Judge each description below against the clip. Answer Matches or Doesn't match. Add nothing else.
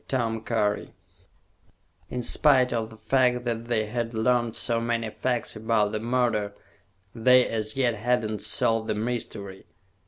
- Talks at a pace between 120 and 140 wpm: Matches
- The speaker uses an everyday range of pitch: Doesn't match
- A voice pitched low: Matches